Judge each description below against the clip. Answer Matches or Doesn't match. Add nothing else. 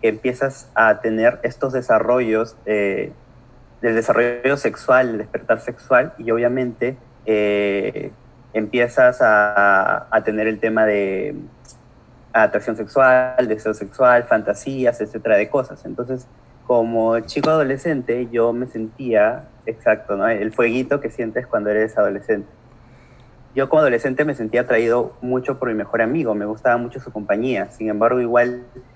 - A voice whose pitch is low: Matches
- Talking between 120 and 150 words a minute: Matches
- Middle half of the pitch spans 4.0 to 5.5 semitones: Doesn't match